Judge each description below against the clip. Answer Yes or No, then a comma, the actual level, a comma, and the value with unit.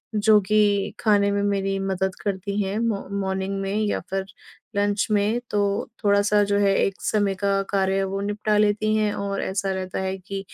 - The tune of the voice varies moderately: No, narrow, 1.1 semitones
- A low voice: No, high, 200 Hz